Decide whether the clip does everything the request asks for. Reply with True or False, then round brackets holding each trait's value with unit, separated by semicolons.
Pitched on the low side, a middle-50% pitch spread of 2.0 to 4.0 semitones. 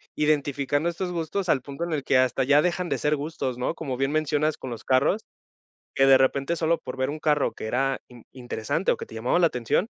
False (145 Hz; 3.6 semitones)